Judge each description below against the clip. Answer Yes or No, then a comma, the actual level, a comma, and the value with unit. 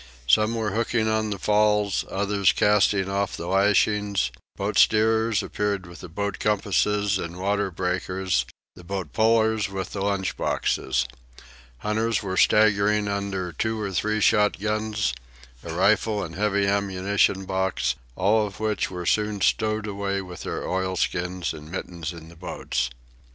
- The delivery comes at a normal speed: Yes, average, 145 wpm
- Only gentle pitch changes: Yes, narrow, 2.2 semitones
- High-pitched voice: No, low, 100 Hz